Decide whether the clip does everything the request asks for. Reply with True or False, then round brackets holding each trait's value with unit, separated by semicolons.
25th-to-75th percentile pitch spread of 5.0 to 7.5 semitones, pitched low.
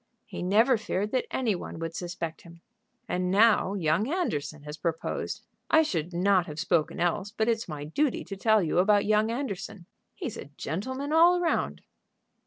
False (5.3 semitones; 195 Hz)